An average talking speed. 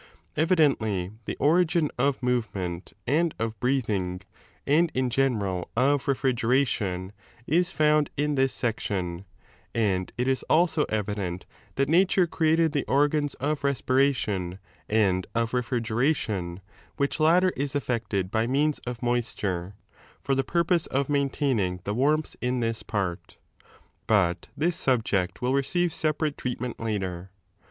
No: slow, 130 wpm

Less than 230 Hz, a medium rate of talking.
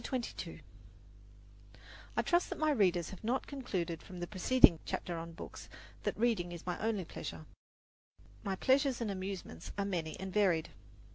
Yes: high, 190 Hz; average, 160 wpm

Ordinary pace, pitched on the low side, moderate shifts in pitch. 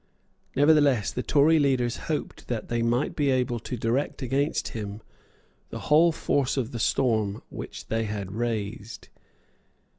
Yes: average, 145 wpm; low, 120 Hz; average, 4.1 semitones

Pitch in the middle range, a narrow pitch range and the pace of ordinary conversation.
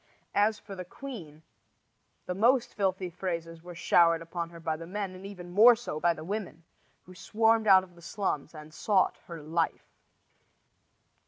No: medium, 180 Hz; average, 3.5 semitones; average, 170 wpm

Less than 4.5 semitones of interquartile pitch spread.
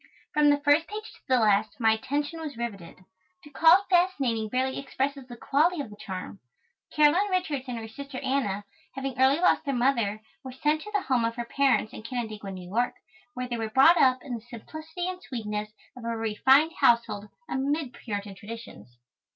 No: average, 4.9 semitones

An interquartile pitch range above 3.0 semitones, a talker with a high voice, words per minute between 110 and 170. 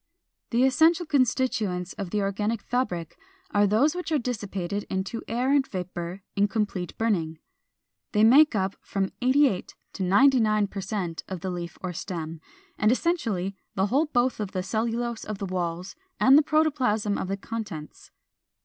Yes: average, 5.1 semitones; high, 210 Hz; average, 160 wpm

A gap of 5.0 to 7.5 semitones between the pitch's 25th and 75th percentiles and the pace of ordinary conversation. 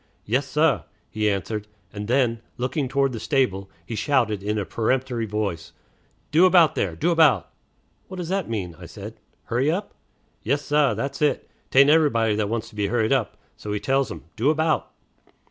Yes: wide, 5.4 semitones; average, 180 wpm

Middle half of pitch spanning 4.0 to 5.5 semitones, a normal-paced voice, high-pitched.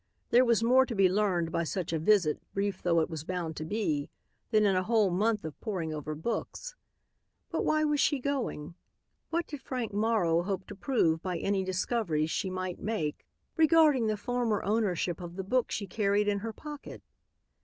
Yes: average, 5.1 semitones; average, 190 wpm; high, 200 Hz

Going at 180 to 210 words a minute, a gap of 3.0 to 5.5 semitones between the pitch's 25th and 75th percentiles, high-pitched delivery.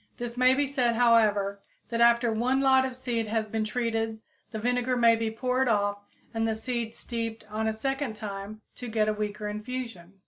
No: average, 185 wpm; narrow, 2.5 semitones; high, 230 Hz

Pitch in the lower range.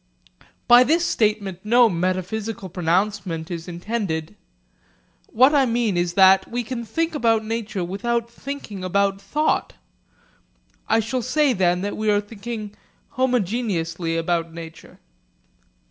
No: high, 210 Hz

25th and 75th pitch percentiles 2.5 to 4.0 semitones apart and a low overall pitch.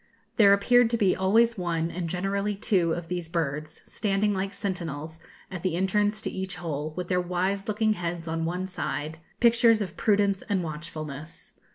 No: average, 3.5 semitones; medium, 185 Hz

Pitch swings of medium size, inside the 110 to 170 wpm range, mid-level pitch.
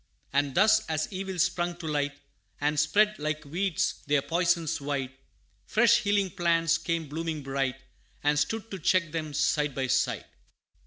Yes: average, 4.1 semitones; average, 155 wpm; medium, 160 Hz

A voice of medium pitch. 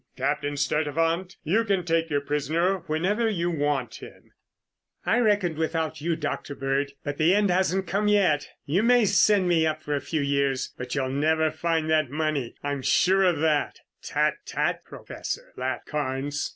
Yes: medium, 160 Hz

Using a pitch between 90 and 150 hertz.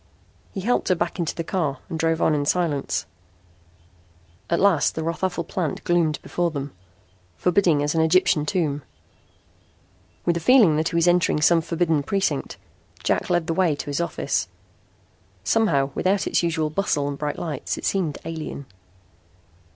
No: medium, 165 Hz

